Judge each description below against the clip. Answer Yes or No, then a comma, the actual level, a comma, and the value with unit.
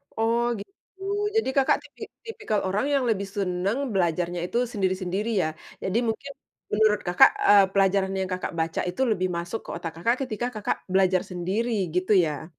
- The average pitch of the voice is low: No, high, 195 Hz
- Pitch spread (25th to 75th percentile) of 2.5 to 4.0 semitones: Yes, average, 3.5 semitones